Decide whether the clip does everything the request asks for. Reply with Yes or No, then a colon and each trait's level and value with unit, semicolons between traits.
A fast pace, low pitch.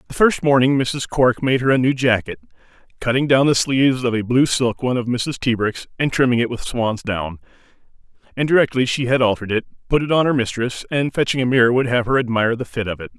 Yes: fast, 230 wpm; low, 125 Hz